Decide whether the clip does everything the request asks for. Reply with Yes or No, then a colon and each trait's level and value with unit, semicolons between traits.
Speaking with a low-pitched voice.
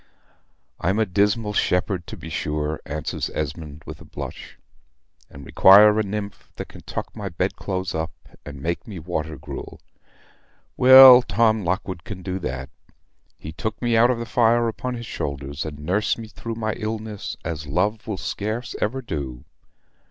Yes: very low, 95 Hz